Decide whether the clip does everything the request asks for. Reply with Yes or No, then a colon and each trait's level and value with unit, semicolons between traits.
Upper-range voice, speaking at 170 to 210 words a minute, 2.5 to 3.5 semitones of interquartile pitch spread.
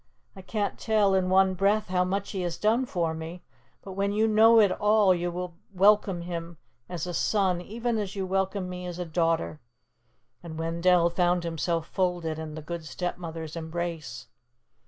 No: medium, 180 Hz; average, 180 wpm; average, 2.8 semitones